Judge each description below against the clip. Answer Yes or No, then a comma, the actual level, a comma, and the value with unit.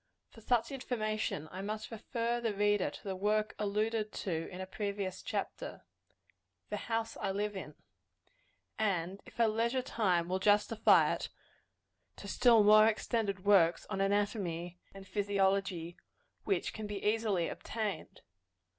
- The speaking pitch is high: Yes, high, 205 Hz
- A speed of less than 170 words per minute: Yes, average, 140 wpm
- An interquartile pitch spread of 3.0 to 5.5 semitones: No, narrow, 2.4 semitones